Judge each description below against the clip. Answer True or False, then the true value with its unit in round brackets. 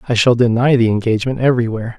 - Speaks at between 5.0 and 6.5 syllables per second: False (7.7 syllables/s)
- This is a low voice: True (120 Hz)